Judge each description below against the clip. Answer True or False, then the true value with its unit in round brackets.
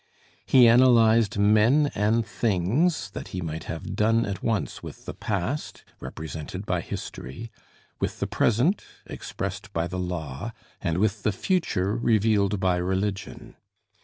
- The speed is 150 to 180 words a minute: False (135 wpm)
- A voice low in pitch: True (105 Hz)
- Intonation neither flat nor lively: True (3.9 semitones)